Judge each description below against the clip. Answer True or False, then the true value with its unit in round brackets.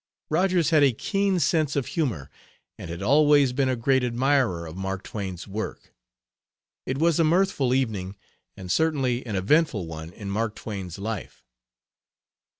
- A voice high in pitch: False (125 Hz)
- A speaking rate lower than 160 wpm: True (150 wpm)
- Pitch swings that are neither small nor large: False (7.5 semitones)